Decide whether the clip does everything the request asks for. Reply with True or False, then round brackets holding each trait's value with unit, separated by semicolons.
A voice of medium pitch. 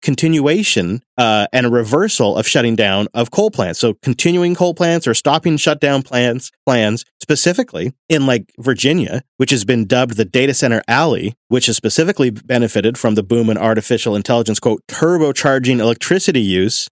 False (130 Hz)